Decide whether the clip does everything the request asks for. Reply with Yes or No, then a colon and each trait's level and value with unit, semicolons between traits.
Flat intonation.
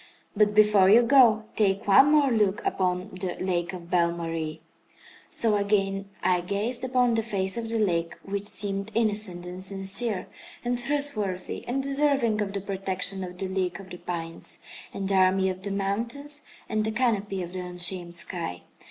No: average, 3.3 semitones